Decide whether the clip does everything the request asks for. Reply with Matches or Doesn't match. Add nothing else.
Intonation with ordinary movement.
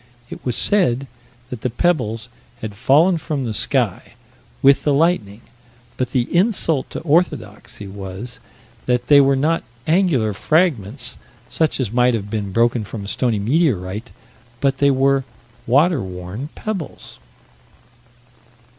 Doesn't match